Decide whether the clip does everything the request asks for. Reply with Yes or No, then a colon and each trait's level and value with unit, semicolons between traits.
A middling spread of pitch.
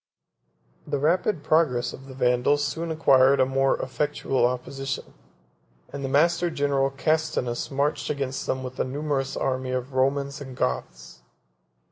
No: narrow, 2.0 semitones